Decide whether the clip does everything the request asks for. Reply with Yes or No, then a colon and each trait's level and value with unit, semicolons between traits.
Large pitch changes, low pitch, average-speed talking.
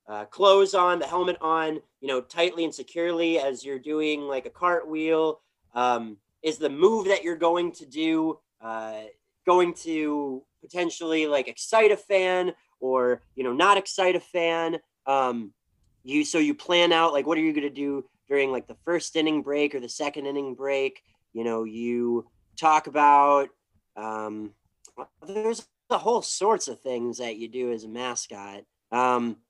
No: wide, 5.9 semitones; medium, 145 Hz; average, 170 wpm